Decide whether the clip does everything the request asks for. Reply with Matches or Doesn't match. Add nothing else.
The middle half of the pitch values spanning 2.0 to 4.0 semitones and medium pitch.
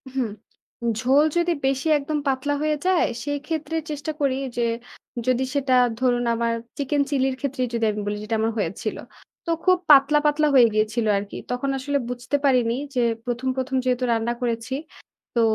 Doesn't match